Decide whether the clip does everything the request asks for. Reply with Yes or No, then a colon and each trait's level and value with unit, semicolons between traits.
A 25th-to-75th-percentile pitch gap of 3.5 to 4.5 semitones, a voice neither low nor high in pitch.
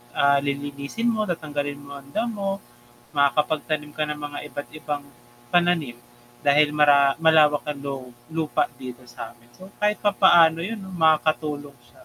No: narrow, 2.6 semitones; medium, 150 Hz